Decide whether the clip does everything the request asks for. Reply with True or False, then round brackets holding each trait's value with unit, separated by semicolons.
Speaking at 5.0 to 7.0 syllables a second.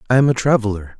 False (7.6 syllables/s)